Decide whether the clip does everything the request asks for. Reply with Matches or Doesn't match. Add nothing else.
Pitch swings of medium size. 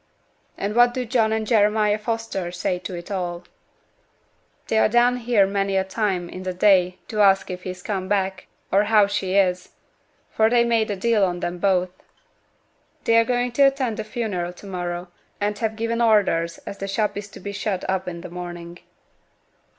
Matches